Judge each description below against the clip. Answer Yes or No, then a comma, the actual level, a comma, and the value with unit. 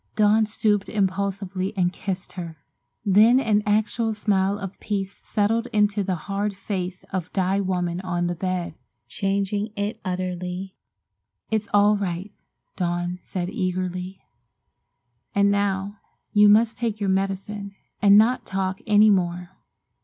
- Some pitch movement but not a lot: No, narrow, 2.1 semitones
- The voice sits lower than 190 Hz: No, high, 195 Hz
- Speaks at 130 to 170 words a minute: Yes, slow, 135 wpm